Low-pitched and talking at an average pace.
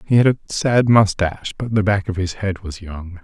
No: low, 100 Hz; fast, 240 wpm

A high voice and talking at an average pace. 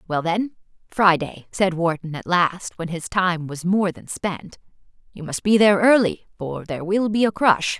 No: medium, 180 Hz; average, 185 wpm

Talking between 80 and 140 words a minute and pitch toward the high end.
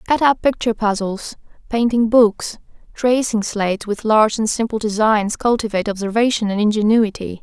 Yes: slow, 135 wpm; high, 220 Hz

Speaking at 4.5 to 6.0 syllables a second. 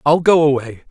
Yes: 5.8 syllables/s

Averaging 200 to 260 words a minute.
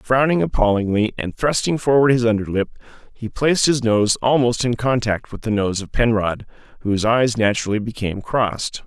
No: average, 160 wpm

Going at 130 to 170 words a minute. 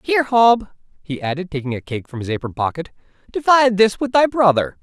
No: average, 200 wpm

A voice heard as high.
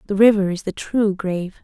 Yes: high, 200 Hz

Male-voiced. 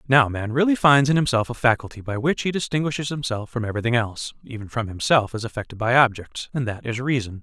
Yes: male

